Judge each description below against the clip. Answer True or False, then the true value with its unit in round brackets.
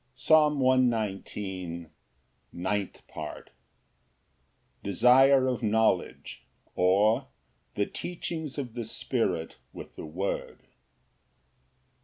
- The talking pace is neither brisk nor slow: False (80 wpm)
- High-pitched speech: False (110 Hz)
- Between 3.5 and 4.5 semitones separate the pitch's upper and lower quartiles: False (5.4 semitones)